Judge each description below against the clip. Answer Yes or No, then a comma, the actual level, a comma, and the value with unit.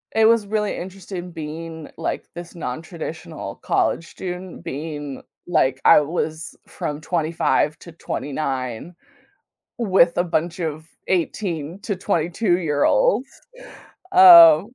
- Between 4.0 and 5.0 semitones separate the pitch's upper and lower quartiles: No, average, 3.3 semitones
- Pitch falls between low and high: Yes, medium, 170 Hz